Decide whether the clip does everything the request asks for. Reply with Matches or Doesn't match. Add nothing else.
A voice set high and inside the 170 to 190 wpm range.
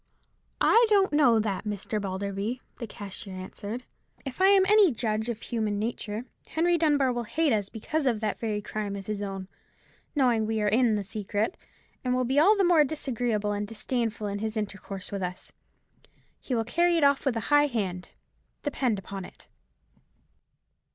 Matches